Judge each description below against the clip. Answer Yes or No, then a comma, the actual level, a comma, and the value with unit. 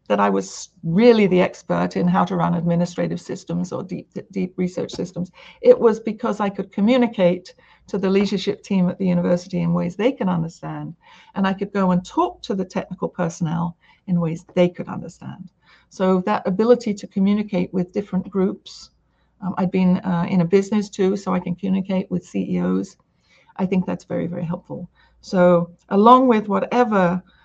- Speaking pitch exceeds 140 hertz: Yes, medium, 185 Hz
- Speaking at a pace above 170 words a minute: Yes, average, 180 wpm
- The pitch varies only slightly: Yes, narrow, 2.2 semitones